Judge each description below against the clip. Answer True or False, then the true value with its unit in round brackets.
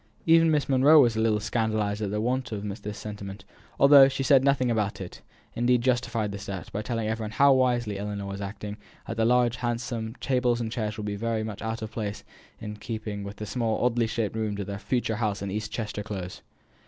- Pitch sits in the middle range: False (110 Hz)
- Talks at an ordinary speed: False (215 wpm)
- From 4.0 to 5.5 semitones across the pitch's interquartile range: False (2.7 semitones)